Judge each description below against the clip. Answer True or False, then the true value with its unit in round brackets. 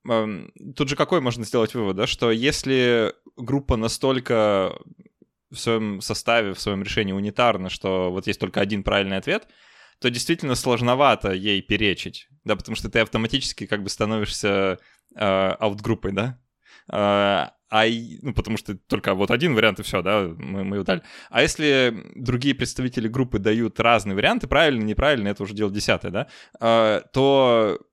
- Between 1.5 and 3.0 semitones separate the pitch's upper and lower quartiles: False (3.4 semitones)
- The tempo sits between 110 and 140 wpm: False (155 wpm)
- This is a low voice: True (110 Hz)